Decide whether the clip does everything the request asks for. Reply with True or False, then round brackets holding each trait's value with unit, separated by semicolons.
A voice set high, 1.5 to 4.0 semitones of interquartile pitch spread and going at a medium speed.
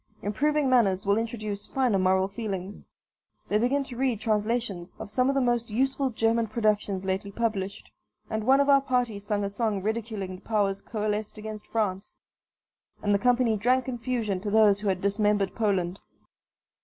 True (215 Hz; 3.2 semitones; 170 wpm)